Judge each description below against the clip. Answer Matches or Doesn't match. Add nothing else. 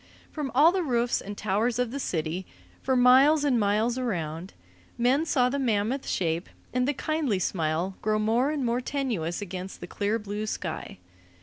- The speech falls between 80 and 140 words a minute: Doesn't match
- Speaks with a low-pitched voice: Doesn't match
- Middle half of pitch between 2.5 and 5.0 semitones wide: Doesn't match